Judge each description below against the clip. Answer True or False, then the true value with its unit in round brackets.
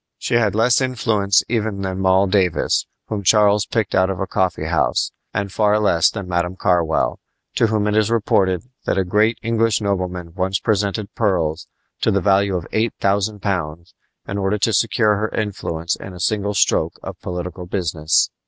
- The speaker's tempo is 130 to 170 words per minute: False (180 wpm)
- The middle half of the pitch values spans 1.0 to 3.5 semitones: True (2.6 semitones)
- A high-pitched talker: False (100 Hz)